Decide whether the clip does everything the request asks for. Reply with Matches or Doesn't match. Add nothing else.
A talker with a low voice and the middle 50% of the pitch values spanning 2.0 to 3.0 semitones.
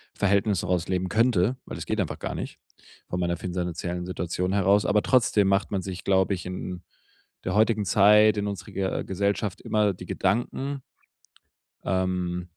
Matches